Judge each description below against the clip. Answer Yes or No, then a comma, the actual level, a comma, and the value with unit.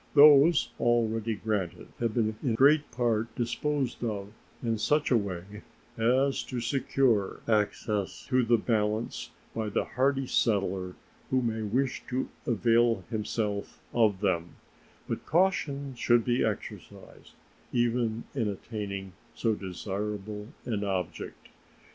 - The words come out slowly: Yes, slow, 125 wpm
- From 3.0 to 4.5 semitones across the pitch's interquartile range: Yes, average, 3.3 semitones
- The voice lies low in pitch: Yes, low, 115 Hz